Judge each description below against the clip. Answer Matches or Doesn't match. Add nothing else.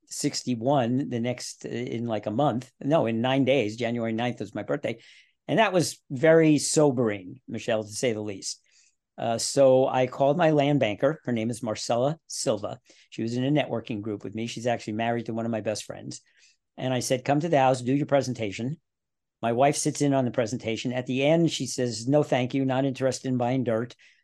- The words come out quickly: Matches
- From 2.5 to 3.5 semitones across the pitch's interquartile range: Matches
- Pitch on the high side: Doesn't match